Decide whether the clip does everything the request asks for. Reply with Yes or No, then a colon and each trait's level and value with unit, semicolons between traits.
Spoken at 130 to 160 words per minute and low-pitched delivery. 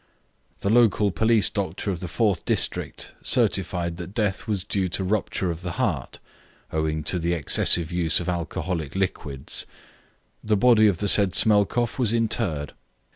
Yes: average, 155 wpm; very low, 95 Hz